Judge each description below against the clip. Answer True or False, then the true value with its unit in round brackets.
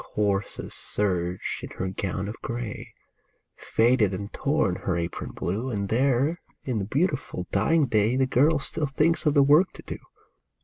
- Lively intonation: True (6.1 semitones)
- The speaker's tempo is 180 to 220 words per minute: False (165 wpm)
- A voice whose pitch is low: True (115 Hz)